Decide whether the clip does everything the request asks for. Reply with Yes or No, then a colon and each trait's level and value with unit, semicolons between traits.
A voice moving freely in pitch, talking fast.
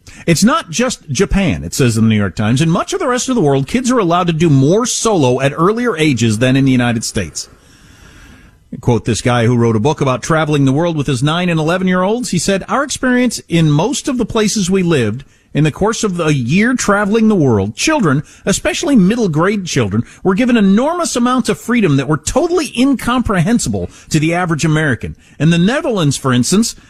Yes: wide, 8.6 semitones; fast, 210 wpm